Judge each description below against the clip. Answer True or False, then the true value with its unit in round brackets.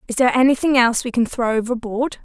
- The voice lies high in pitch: True (240 Hz)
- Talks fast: True (215 wpm)